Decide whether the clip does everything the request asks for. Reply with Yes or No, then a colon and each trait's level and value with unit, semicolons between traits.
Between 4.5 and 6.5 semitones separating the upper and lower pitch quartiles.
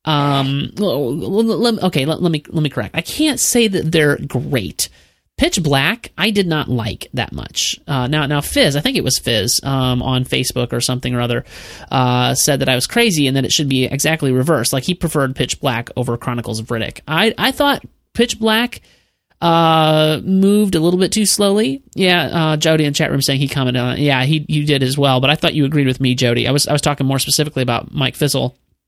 Yes: average, 4.8 semitones